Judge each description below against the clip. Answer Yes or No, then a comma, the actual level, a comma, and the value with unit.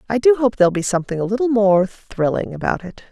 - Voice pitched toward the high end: Yes, high, 210 Hz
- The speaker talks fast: Yes, fast, 230 wpm